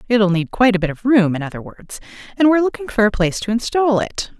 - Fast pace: Yes, fast, 260 wpm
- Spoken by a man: No, female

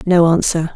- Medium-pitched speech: Yes, medium, 170 Hz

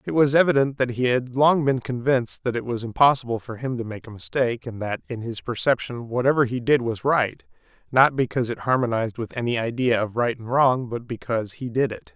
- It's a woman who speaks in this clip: No, male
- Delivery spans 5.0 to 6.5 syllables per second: Yes, 5.8 syllables/s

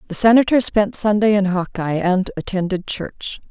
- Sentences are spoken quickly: No, average, 155 wpm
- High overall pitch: Yes, high, 200 Hz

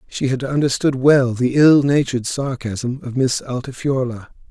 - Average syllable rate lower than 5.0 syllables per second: Yes, 4.5 syllables/s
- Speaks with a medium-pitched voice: No, low, 130 Hz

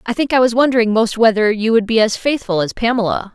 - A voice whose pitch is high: Yes, high, 225 Hz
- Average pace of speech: No, fast, 250 wpm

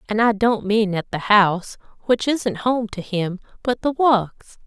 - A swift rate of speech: No, average, 195 wpm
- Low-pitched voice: No, high, 215 Hz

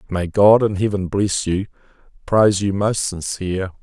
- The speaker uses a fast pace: No, average, 155 wpm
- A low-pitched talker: Yes, low, 100 Hz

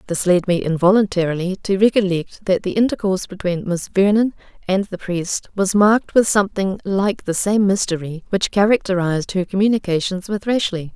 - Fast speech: No, average, 160 wpm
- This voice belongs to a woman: Yes, female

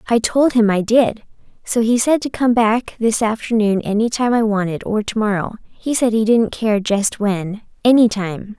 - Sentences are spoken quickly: No, average, 180 wpm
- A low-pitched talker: No, high, 220 Hz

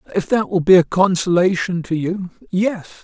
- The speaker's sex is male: Yes, male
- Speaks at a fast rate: No, average, 180 wpm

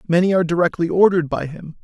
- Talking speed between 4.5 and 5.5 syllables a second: No, 7.3 syllables/s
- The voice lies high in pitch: No, medium, 170 Hz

